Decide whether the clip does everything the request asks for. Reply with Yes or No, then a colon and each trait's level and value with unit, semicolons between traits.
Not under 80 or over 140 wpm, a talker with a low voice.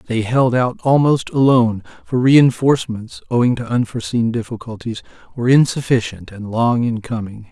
Yes: slow, 135 wpm; low, 120 Hz